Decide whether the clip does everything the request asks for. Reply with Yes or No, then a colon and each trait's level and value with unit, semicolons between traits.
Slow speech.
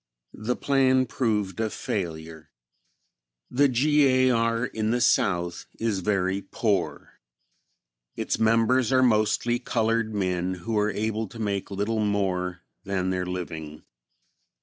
Yes: slow, 125 wpm